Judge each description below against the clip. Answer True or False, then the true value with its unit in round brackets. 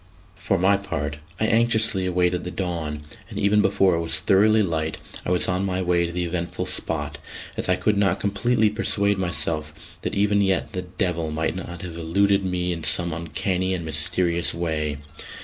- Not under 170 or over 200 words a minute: True (185 wpm)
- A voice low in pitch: True (90 Hz)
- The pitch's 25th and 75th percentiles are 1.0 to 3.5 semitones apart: True (2.9 semitones)